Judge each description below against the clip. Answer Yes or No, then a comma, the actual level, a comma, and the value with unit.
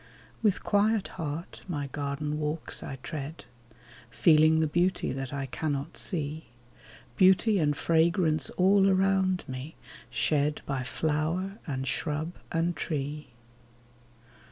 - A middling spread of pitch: Yes, average, 3.9 semitones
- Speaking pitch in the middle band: Yes, medium, 155 Hz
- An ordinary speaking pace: No, slow, 115 wpm